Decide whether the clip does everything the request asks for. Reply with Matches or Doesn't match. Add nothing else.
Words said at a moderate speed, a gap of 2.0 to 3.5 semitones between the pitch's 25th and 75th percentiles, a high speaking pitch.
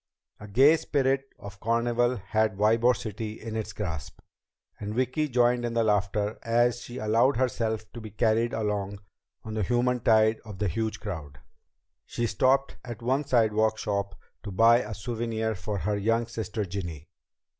Doesn't match